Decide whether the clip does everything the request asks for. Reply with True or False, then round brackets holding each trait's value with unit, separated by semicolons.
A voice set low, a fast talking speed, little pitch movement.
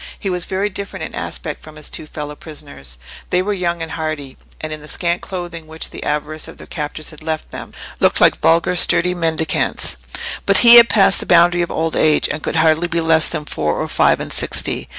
False (160 Hz; 220 wpm; 2.3 semitones)